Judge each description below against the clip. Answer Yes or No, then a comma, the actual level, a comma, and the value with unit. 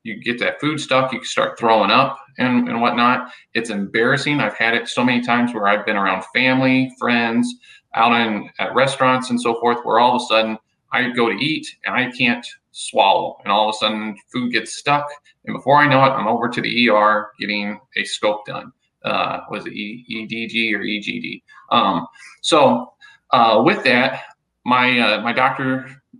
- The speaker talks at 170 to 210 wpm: Yes, fast, 205 wpm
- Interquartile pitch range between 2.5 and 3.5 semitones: Yes, average, 3.2 semitones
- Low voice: Yes, low, 120 Hz